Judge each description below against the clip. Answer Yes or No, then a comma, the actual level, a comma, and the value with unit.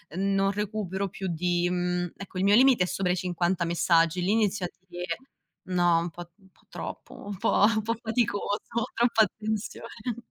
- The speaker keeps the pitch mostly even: No, average, 3.1 semitones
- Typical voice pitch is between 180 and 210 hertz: Yes, high, 190 Hz